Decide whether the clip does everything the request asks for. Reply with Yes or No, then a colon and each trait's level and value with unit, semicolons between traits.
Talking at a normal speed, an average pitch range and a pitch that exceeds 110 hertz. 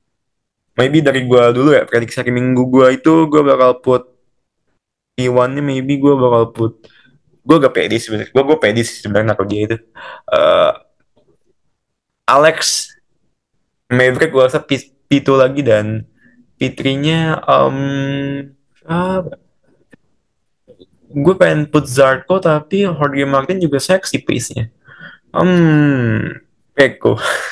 Yes: average, 120 wpm; average, 3.7 semitones; low, 135 Hz